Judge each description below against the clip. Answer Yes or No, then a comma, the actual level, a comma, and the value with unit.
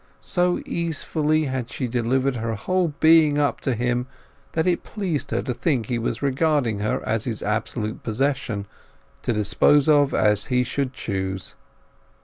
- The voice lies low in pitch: Yes, low, 130 Hz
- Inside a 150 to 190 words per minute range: Yes, average, 155 wpm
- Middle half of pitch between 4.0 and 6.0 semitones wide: Yes, average, 4.9 semitones